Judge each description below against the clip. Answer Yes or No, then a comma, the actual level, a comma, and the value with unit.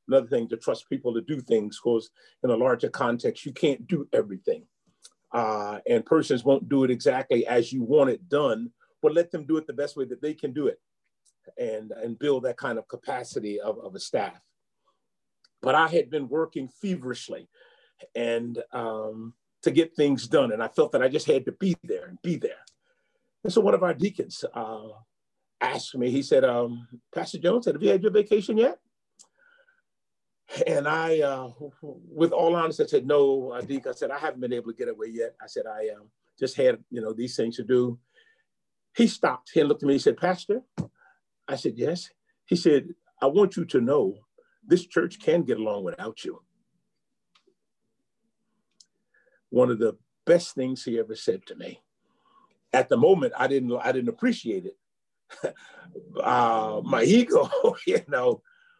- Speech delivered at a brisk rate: No, average, 185 wpm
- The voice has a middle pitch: Yes, medium, 165 Hz